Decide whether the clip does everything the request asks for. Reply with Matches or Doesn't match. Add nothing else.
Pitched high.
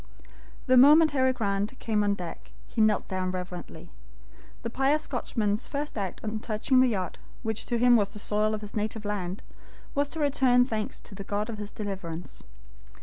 Matches